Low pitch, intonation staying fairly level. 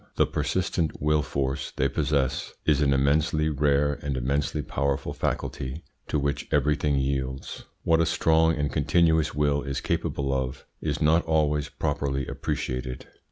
Yes: very low, 70 Hz; narrow, 2.1 semitones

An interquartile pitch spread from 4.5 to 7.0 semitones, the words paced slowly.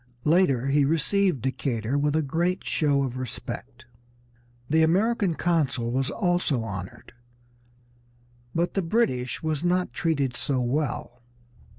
Yes: average, 5.2 semitones; slow, 120 wpm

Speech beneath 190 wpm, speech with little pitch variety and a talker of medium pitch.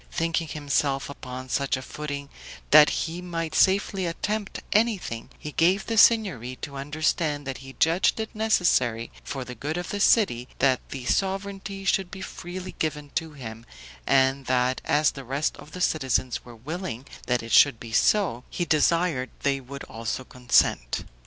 No: average, 165 wpm; wide, 5.6 semitones; medium, 150 Hz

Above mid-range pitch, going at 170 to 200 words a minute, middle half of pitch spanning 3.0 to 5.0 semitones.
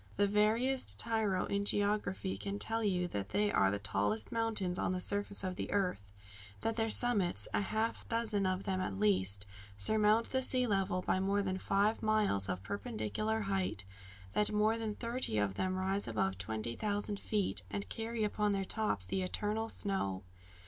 Yes: high, 200 Hz; average, 175 wpm; average, 3.6 semitones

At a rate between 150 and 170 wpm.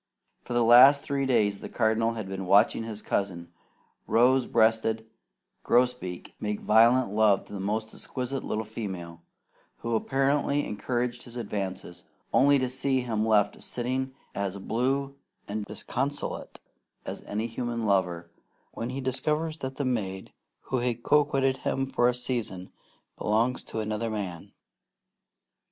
No: average, 140 wpm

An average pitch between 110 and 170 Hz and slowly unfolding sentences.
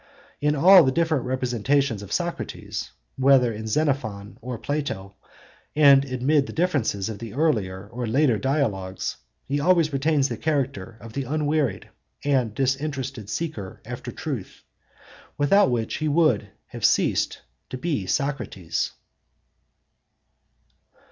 Yes: low, 135 Hz; slow, 125 wpm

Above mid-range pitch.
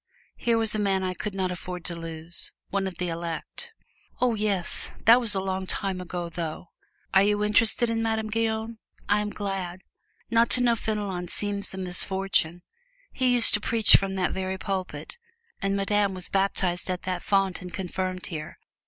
Yes: high, 195 Hz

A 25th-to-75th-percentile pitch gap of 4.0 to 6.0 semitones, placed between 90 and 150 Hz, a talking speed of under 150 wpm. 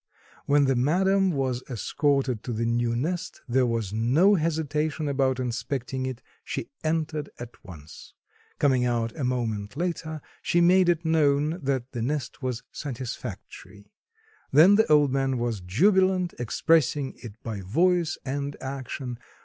Yes: average, 4.7 semitones; low, 135 Hz; average, 140 wpm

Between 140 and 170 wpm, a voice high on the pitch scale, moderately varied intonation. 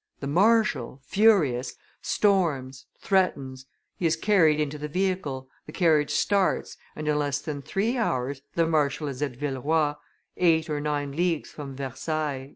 No: average, 150 wpm; medium, 150 Hz; average, 3.9 semitones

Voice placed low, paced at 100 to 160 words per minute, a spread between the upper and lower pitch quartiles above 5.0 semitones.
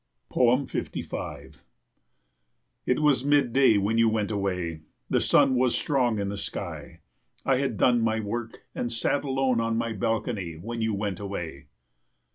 No: low, 115 Hz; average, 150 wpm; average, 3.9 semitones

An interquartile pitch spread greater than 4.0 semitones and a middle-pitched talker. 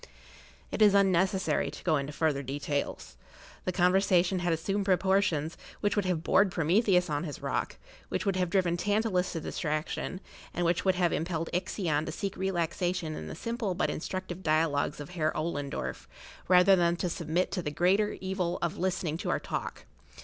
No: average, 3.1 semitones; medium, 175 Hz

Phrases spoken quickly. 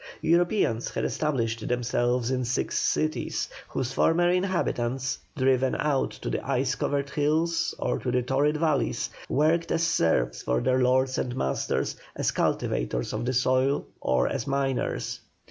No: average, 145 wpm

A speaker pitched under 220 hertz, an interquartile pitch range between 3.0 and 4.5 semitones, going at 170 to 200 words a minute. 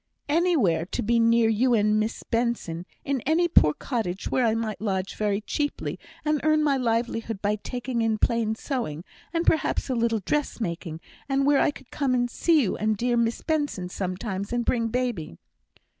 No: high, 230 Hz; average, 4.2 semitones; average, 180 wpm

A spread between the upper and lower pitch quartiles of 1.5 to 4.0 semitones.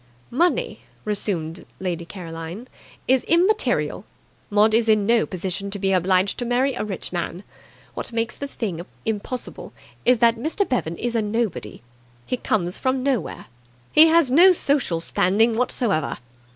No: average, 5.3 semitones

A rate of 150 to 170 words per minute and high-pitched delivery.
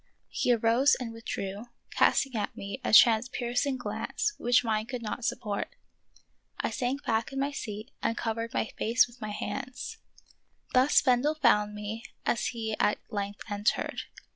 Yes: average, 155 wpm; high, 230 Hz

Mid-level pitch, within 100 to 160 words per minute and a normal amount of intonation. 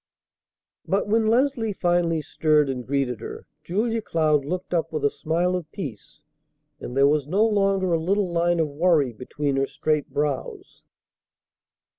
Yes: medium, 165 Hz; average, 155 wpm; average, 4.7 semitones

